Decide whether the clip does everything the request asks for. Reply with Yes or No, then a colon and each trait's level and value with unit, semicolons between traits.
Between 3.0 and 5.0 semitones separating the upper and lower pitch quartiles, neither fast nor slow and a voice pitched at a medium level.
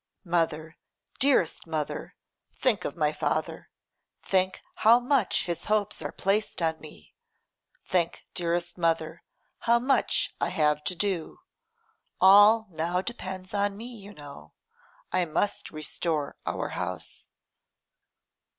No: average, 4.1 semitones; slow, 120 wpm; medium, 180 Hz